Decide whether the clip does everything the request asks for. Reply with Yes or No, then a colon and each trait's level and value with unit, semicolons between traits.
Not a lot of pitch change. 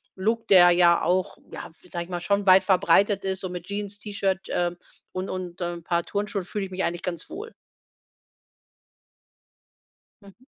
Yes: narrow, 2.3 semitones